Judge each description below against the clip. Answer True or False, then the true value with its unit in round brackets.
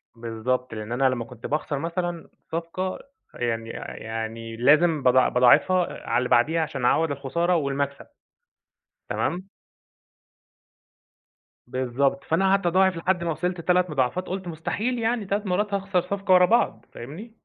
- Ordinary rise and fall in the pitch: False (6.3 semitones)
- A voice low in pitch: False (165 Hz)